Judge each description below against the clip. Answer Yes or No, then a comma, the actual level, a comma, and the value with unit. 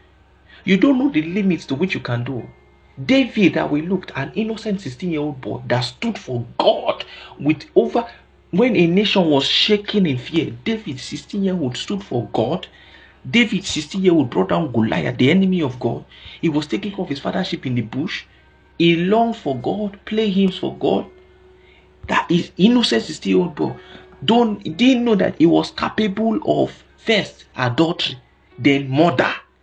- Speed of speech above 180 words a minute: No, average, 175 wpm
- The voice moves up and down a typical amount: No, wide, 7.7 semitones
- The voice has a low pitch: No, medium, 170 Hz